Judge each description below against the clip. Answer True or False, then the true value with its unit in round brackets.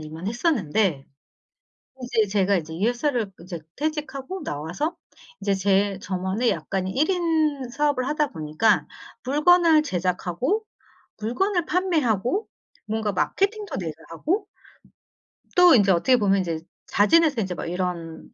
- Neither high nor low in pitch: False (220 Hz)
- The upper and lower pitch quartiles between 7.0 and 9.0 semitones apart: True (8.7 semitones)